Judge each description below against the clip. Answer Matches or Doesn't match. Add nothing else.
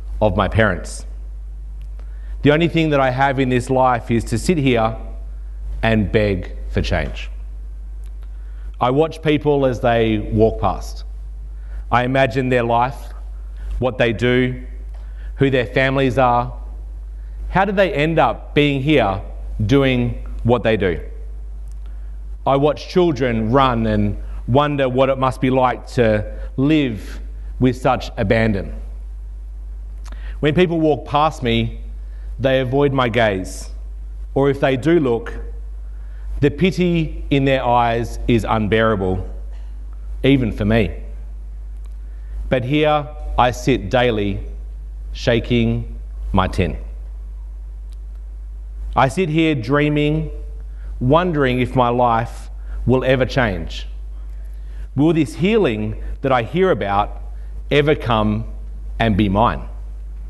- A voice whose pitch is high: Doesn't match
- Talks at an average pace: Doesn't match